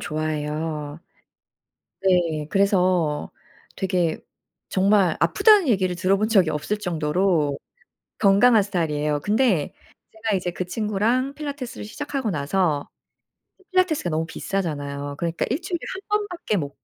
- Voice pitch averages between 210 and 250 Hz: No, medium, 185 Hz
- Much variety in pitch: Yes, wide, 5.8 semitones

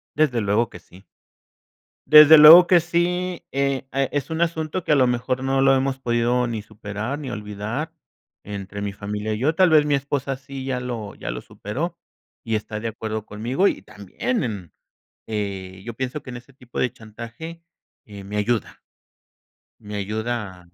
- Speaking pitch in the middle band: No, low, 120 Hz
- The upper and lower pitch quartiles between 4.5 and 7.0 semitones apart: Yes, average, 4.9 semitones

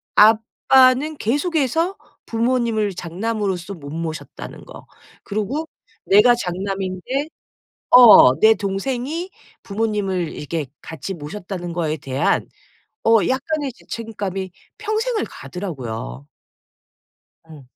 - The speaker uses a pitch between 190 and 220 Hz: Yes, high, 210 Hz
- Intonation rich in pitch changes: Yes, wide, 6.4 semitones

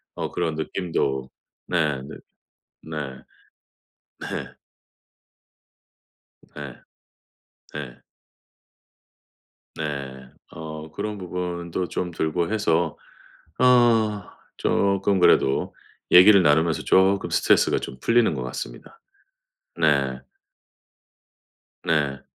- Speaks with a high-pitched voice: No, very low, 80 Hz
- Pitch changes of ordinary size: Yes, average, 4.8 semitones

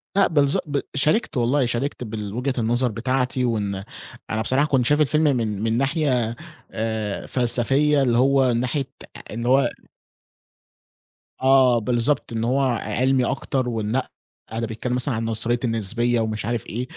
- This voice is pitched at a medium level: No, low, 125 Hz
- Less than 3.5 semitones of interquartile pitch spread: Yes, average, 3.0 semitones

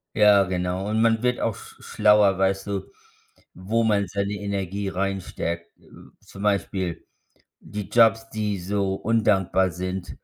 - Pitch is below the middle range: Yes, low, 100 Hz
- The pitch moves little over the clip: Yes, narrow, 1.9 semitones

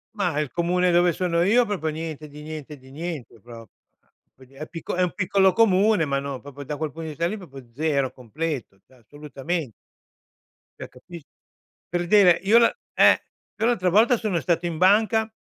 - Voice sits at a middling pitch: Yes, medium, 165 Hz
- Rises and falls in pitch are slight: No, average, 4.5 semitones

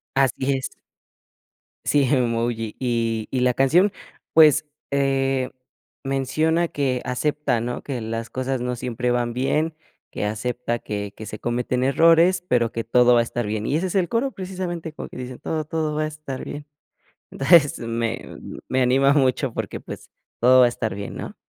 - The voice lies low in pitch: Yes, low, 130 Hz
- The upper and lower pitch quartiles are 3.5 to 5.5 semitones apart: Yes, average, 4.1 semitones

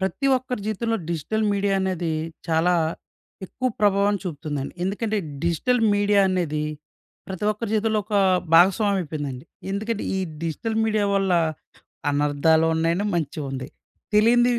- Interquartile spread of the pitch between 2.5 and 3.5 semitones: No, average, 4.9 semitones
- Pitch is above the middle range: Yes, high, 195 Hz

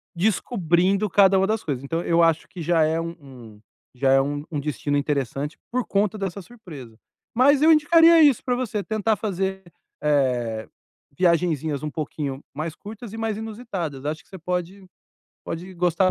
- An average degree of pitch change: No, wide, 6.1 semitones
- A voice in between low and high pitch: Yes, medium, 175 Hz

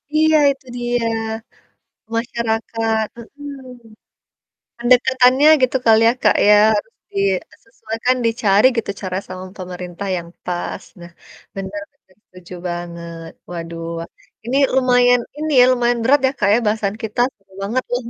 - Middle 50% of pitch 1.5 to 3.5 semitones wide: No, average, 4.9 semitones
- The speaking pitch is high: Yes, high, 225 Hz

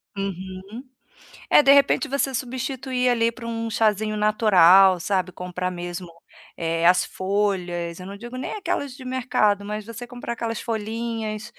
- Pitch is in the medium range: No, high, 215 Hz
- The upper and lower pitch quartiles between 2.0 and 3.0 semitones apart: No, average, 4.4 semitones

